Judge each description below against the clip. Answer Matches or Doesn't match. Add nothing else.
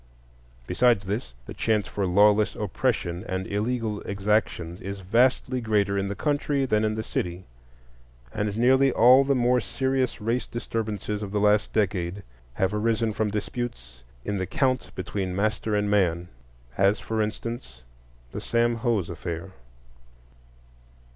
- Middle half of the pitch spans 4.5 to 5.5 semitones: Doesn't match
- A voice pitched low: Matches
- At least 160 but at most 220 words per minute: Doesn't match